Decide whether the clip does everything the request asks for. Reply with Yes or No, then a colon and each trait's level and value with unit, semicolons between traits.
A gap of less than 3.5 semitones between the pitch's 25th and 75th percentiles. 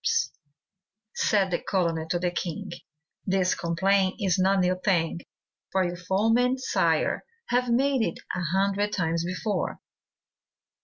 Yes: average, 2.8 semitones